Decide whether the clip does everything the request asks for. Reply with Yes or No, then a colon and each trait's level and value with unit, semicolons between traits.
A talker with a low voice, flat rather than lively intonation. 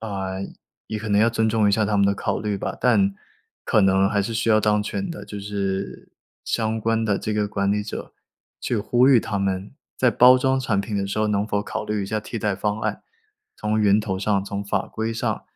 Yes: low, 105 Hz; narrow, 1.9 semitones